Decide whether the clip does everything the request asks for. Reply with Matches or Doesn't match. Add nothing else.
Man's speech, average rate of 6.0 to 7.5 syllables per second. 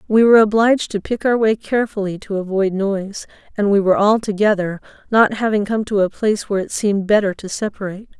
Doesn't match